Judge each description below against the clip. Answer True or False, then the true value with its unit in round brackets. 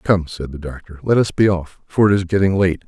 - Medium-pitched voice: False (90 Hz)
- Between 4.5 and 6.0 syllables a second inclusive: True (5.5 syllables/s)